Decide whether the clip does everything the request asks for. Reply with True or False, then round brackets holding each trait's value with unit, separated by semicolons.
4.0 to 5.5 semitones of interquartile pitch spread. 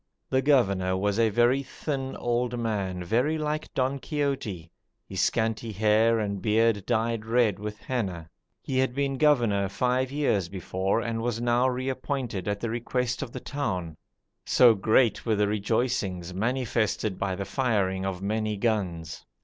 True (4.3 semitones)